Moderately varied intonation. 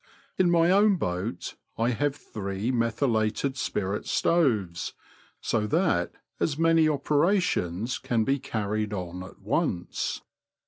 No: wide, 7.5 semitones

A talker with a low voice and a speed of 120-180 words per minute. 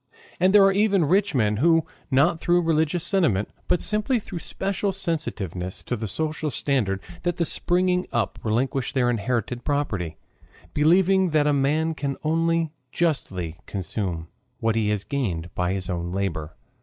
No: medium, 145 Hz; average, 155 wpm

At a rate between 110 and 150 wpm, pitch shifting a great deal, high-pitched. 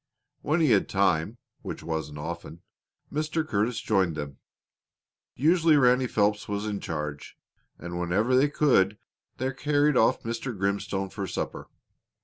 No: slow, 135 wpm; wide, 7.0 semitones; low, 105 Hz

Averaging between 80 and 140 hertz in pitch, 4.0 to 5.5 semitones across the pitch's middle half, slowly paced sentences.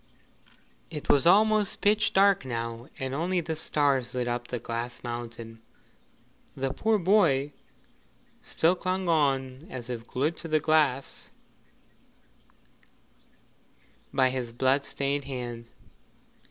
Yes: low, 135 Hz; average, 5.2 semitones; slow, 115 wpm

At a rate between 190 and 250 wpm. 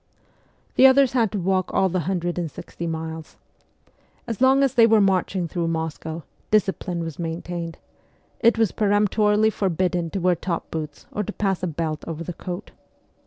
No: average, 170 wpm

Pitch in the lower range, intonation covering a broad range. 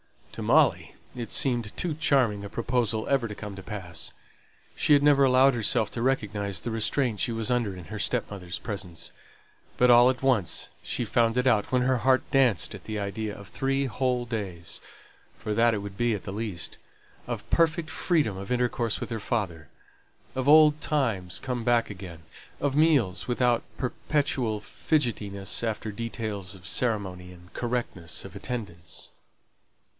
No: low, 115 Hz; average, 4.1 semitones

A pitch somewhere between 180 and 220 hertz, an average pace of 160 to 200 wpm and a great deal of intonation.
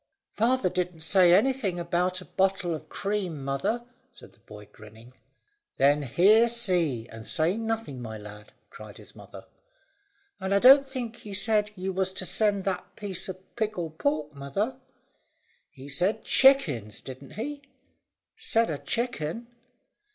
No: medium, 185 Hz; average, 145 wpm; wide, 7.0 semitones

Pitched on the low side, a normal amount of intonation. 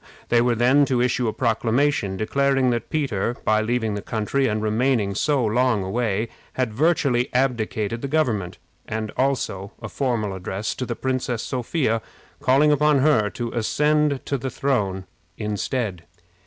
Yes: low, 120 Hz; average, 3.9 semitones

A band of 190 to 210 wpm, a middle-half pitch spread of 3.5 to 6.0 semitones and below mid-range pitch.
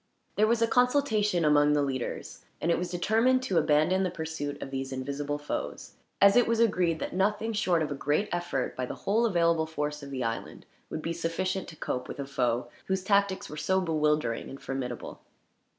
No: average, 200 wpm; wide, 5.4 semitones; medium, 165 Hz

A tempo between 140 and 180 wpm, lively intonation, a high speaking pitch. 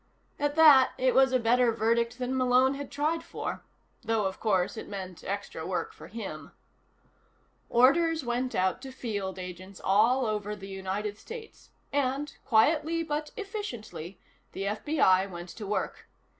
Yes: average, 150 wpm; wide, 5.9 semitones; high, 235 Hz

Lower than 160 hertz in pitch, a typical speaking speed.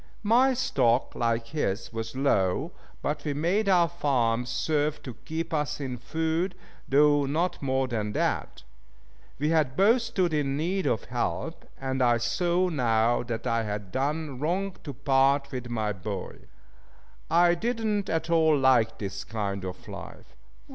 Yes: medium, 140 Hz; average, 155 wpm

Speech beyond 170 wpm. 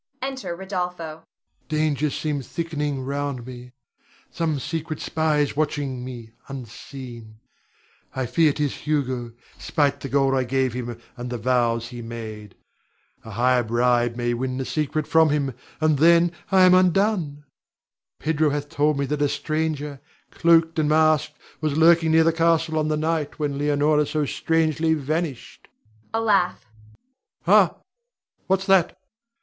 No: average, 145 wpm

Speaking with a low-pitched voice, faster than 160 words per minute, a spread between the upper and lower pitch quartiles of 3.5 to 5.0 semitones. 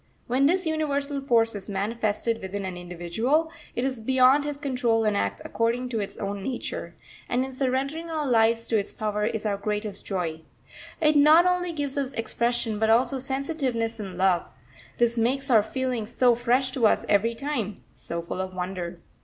No: high, 235 Hz; average, 180 wpm; average, 4.7 semitones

